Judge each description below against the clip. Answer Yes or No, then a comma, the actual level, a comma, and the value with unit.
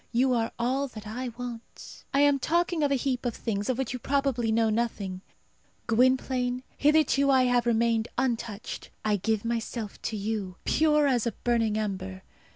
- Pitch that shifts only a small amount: No, average, 3.1 semitones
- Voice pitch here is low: No, high, 240 Hz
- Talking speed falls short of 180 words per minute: Yes, average, 170 wpm